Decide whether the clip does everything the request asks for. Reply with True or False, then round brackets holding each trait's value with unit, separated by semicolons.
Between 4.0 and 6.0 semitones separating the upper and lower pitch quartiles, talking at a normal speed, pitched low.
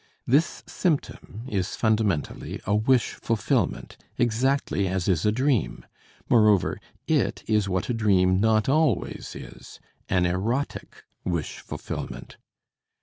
False (4.4 semitones; 115 wpm; 110 Hz)